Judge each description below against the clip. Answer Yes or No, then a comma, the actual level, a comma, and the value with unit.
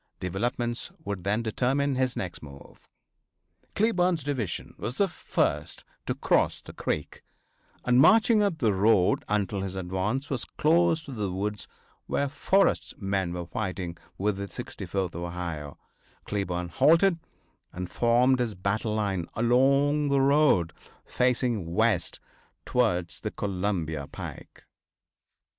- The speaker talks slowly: Yes, slow, 125 wpm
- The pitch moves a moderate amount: No, wide, 6.5 semitones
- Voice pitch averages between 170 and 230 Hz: No, low, 105 Hz